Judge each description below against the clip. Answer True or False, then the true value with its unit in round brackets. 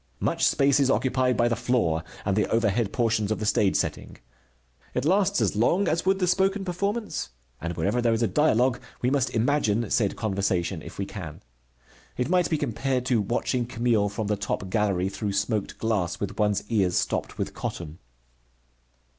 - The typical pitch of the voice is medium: False (115 Hz)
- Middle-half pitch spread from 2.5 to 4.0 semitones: False (4.8 semitones)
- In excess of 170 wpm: True (180 wpm)